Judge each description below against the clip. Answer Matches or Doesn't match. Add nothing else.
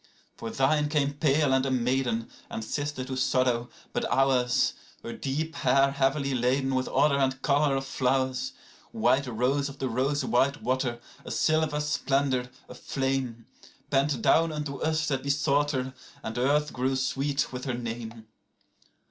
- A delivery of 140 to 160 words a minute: Matches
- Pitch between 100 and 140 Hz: Matches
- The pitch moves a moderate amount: Doesn't match